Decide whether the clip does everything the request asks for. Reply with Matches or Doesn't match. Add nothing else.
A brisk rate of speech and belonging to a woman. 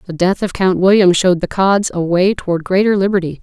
Matches